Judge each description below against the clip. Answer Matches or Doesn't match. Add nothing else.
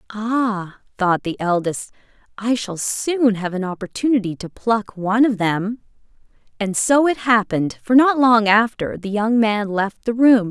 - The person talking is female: Matches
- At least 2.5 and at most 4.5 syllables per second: Matches